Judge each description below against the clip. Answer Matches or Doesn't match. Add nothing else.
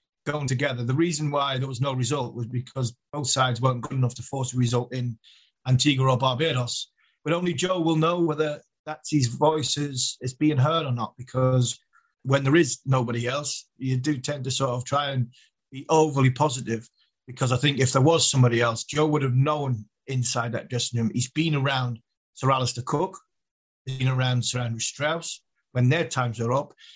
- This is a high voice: Doesn't match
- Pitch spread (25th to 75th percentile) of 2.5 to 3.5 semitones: Matches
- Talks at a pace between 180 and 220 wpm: Matches